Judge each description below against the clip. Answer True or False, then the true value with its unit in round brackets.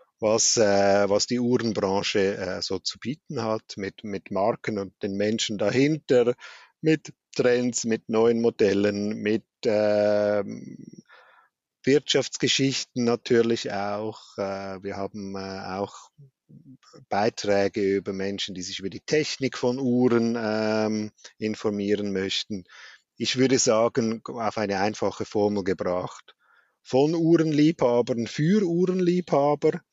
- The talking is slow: True (115 wpm)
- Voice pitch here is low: True (110 Hz)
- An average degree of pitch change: True (4.1 semitones)